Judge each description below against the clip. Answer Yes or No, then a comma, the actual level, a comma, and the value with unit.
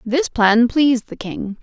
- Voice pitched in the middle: No, high, 240 Hz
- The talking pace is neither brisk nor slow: Yes, average, 185 wpm